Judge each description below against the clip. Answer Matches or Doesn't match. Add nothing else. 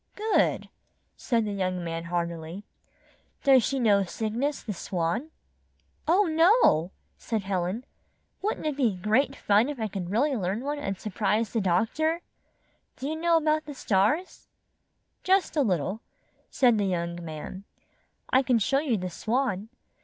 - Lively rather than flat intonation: Matches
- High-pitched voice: Matches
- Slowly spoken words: Doesn't match